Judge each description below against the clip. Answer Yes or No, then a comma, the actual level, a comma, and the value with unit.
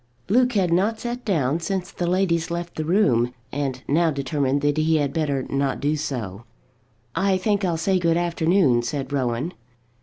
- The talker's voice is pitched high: No, medium, 160 Hz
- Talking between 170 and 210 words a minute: Yes, average, 175 wpm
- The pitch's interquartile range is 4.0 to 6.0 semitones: Yes, average, 4.9 semitones